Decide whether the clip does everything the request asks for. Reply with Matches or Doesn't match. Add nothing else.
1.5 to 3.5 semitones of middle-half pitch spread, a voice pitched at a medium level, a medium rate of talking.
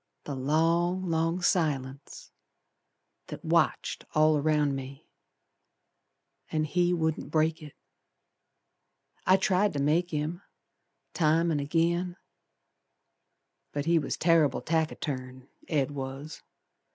Doesn't match